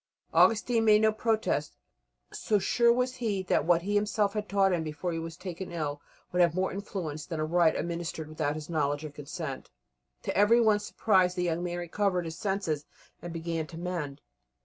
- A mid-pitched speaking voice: Yes, medium, 175 Hz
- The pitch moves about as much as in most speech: Yes, average, 4.3 semitones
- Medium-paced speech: Yes, average, 190 wpm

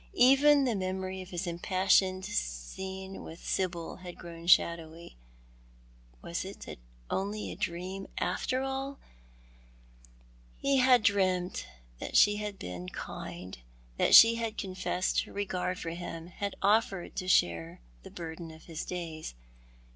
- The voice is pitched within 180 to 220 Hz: Yes, medium, 185 Hz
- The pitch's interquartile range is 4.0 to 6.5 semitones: No, average, 3.2 semitones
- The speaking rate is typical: No, slow, 130 wpm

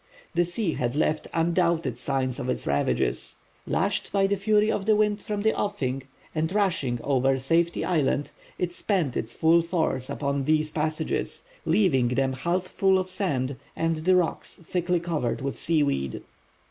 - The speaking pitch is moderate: Yes, medium, 160 Hz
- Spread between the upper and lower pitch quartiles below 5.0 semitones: No, wide, 5.4 semitones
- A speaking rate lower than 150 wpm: No, average, 160 wpm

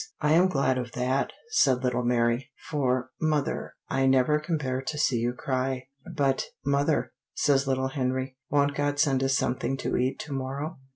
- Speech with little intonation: Yes, narrow, 1.9 semitones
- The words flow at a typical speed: Yes, average, 180 wpm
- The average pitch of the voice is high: No, low, 135 Hz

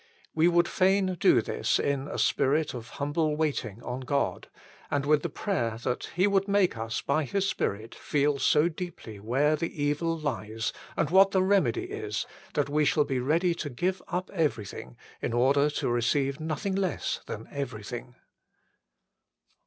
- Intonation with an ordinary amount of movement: No, wide, 5.8 semitones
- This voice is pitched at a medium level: Yes, medium, 150 Hz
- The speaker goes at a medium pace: Yes, average, 165 wpm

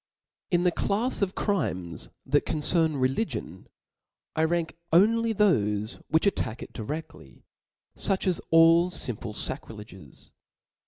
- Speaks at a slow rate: Yes, slow, 115 wpm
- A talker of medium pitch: Yes, medium, 160 Hz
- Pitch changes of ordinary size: No, wide, 9.0 semitones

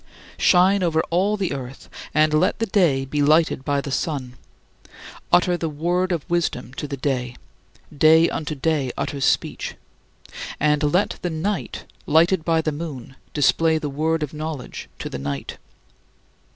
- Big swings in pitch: No, average, 3.2 semitones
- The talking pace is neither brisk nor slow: Yes, average, 155 wpm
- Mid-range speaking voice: Yes, medium, 155 Hz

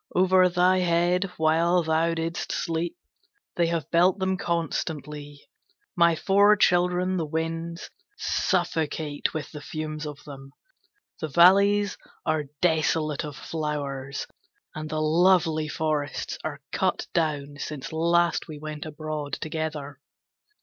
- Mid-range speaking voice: Yes, medium, 160 Hz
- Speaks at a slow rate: Yes, slow, 120 wpm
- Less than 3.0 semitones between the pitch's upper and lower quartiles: Yes, narrow, 2.4 semitones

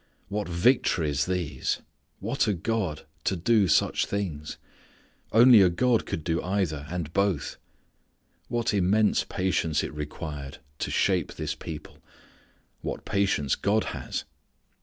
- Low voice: Yes, very low, 90 Hz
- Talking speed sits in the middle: No, slow, 125 wpm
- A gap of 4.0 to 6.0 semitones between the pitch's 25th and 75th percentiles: Yes, average, 5.0 semitones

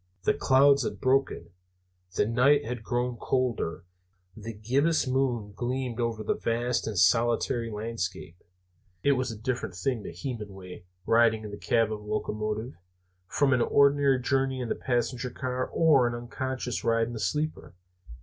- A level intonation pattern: No, average, 3.2 semitones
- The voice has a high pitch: No, low, 120 Hz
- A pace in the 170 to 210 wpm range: No, average, 160 wpm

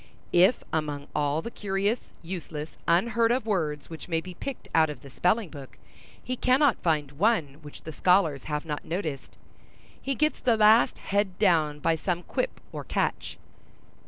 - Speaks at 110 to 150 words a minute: No, average, 165 wpm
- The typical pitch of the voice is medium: Yes, medium, 170 Hz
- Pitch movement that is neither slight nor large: No, wide, 6.3 semitones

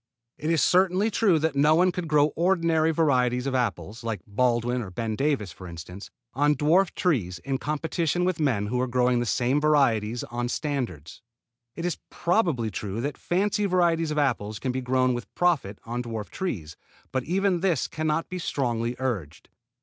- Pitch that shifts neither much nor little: No, wide, 5.9 semitones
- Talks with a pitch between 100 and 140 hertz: Yes, low, 135 Hz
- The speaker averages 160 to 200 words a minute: Yes, average, 180 wpm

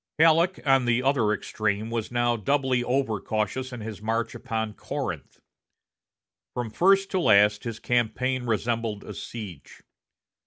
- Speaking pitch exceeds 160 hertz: No, low, 120 Hz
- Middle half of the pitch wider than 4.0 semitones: No, average, 3.3 semitones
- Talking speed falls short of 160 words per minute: Yes, average, 140 wpm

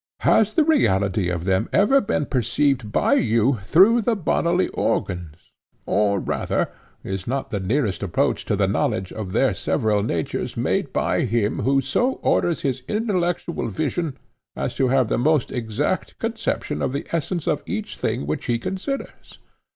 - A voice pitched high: No, low, 125 Hz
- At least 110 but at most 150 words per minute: No, average, 160 wpm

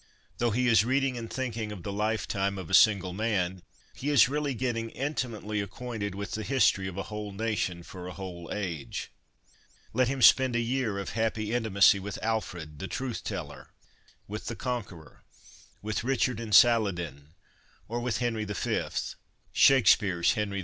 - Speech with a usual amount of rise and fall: Yes, average, 3.7 semitones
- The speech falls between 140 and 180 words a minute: Yes, average, 165 wpm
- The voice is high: No, low, 110 Hz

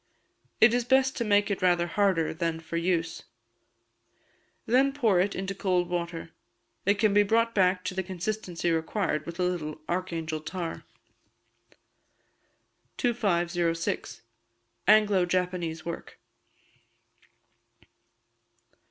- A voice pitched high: No, medium, 180 Hz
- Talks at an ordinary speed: No, slow, 110 wpm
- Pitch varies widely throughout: No, average, 3.4 semitones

